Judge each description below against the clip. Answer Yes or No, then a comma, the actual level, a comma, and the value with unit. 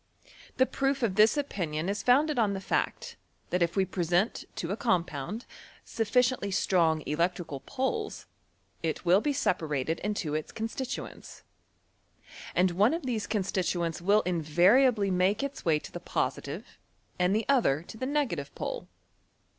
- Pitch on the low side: No, high, 195 Hz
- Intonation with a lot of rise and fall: Yes, wide, 6.2 semitones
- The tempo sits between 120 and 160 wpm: Yes, average, 150 wpm